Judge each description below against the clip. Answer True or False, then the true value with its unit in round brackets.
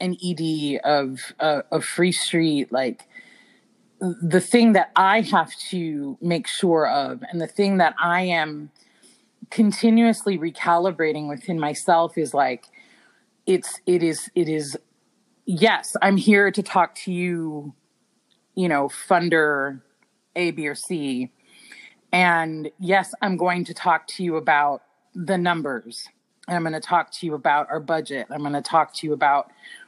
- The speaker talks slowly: False (155 wpm)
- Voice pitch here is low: False (170 Hz)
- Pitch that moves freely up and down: False (4.0 semitones)